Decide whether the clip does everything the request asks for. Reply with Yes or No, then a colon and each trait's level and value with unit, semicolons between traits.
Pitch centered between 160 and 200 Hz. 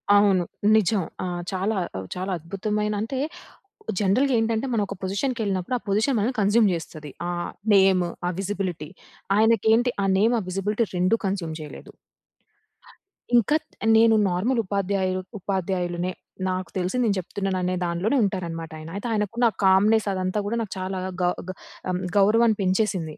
Yes: high, 195 Hz